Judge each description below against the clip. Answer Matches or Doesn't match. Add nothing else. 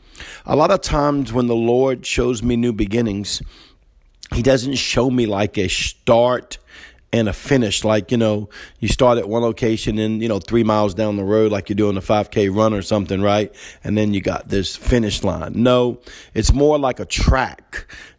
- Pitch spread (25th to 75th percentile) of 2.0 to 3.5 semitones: Matches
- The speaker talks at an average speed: Matches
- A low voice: Matches